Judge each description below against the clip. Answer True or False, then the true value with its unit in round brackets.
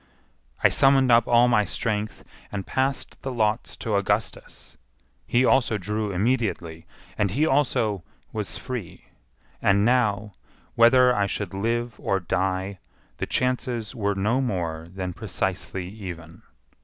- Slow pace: True (130 wpm)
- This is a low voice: True (105 Hz)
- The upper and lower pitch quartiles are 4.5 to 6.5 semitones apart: False (4.1 semitones)